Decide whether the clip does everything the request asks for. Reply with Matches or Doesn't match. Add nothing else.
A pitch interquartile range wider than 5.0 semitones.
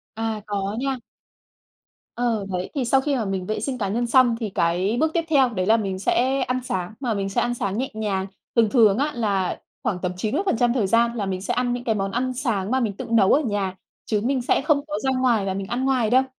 Doesn't match